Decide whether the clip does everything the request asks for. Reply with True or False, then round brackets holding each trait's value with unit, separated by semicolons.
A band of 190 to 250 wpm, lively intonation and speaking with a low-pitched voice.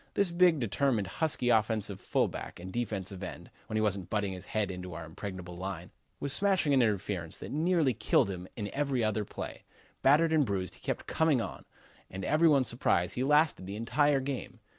True (195 wpm; 6.8 semitones; 110 Hz)